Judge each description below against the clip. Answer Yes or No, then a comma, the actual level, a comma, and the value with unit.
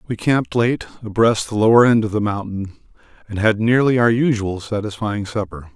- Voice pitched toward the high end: No, low, 110 Hz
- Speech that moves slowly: No, average, 175 wpm